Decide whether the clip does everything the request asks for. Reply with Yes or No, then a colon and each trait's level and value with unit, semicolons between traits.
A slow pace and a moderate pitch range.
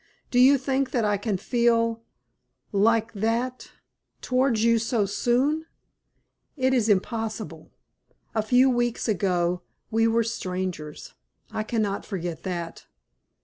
Yes: slow, 120 wpm; average, 3.4 semitones